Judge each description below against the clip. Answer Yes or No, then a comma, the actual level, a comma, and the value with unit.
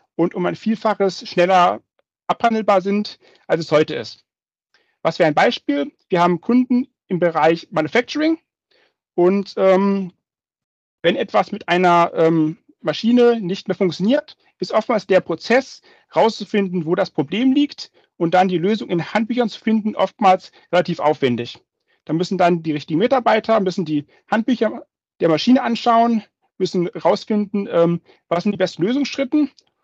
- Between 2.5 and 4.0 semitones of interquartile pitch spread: No, average, 5.0 semitones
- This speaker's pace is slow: No, average, 145 wpm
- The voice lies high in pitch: Yes, high, 195 Hz